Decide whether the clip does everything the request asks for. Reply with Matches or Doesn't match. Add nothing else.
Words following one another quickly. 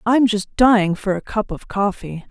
Matches